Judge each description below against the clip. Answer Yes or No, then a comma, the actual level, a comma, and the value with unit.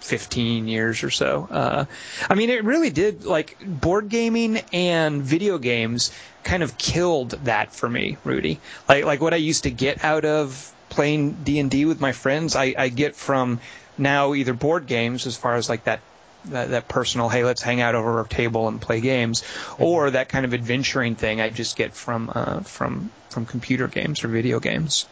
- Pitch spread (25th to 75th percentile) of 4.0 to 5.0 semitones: Yes, average, 4.6 semitones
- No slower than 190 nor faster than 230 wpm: Yes, average, 200 wpm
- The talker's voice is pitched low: Yes, low, 130 Hz